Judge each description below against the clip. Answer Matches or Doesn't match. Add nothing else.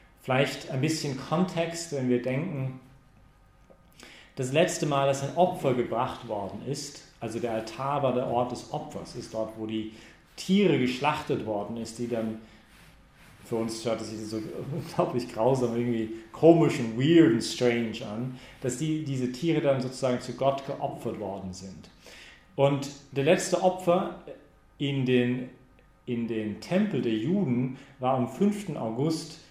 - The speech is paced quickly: Doesn't match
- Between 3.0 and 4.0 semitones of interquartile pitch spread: Doesn't match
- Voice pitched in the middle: Doesn't match